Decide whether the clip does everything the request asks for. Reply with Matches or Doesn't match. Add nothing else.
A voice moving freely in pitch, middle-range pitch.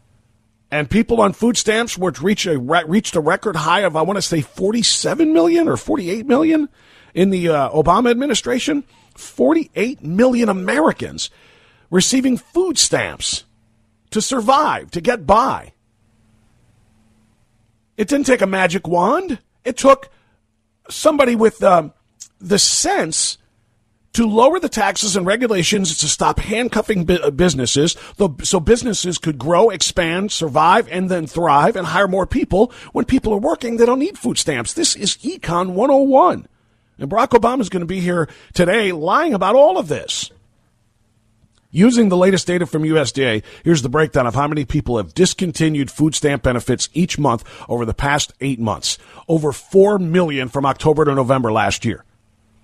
Matches